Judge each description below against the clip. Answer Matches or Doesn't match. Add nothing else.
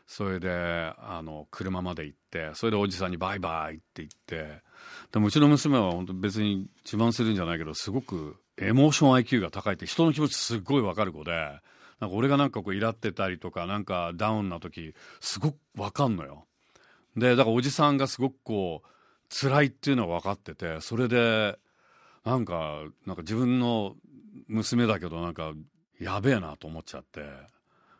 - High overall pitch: Doesn't match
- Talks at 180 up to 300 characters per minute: Doesn't match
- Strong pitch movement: Matches